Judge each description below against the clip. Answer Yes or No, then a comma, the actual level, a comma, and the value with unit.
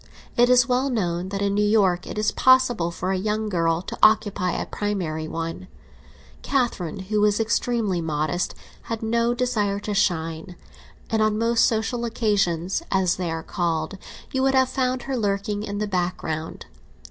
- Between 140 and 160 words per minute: No, average, 170 wpm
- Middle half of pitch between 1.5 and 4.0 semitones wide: No, average, 4.6 semitones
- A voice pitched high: Yes, high, 205 Hz